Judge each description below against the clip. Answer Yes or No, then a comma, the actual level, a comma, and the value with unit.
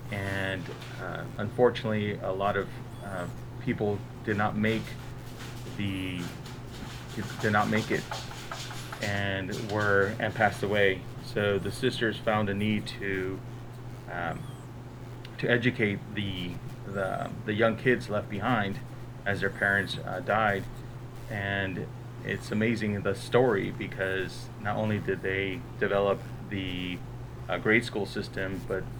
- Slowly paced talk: Yes, slow, 125 wpm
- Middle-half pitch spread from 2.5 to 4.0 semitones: Yes, average, 3.6 semitones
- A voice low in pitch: Yes, low, 115 Hz